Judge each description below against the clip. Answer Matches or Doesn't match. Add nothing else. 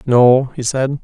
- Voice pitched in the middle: Doesn't match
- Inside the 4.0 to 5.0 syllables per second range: Doesn't match